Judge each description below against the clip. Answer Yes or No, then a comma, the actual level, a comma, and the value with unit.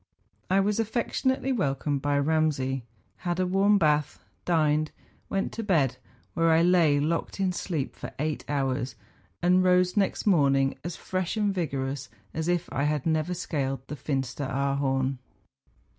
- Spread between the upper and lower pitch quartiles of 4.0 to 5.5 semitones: Yes, average, 4.8 semitones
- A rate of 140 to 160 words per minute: Yes, average, 150 wpm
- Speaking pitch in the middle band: Yes, medium, 155 Hz